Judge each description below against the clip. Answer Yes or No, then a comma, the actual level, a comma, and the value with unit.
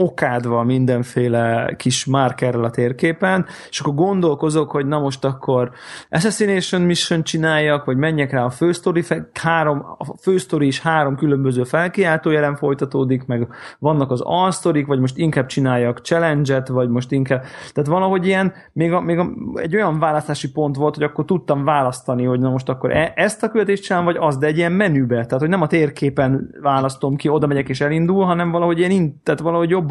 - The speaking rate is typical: No, fast, 180 wpm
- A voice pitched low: No, medium, 150 Hz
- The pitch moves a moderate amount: Yes, average, 4.4 semitones